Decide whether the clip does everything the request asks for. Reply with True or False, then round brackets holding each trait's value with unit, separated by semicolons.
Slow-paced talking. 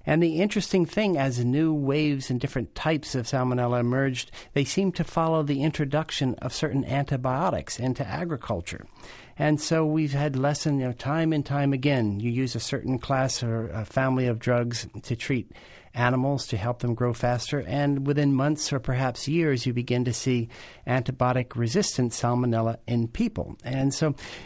False (170 wpm)